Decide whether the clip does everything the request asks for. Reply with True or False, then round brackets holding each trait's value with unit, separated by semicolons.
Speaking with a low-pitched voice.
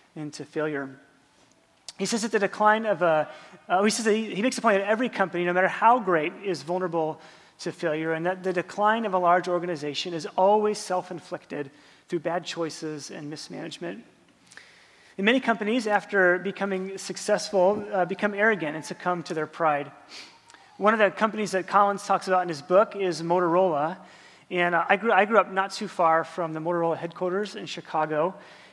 False (180 Hz)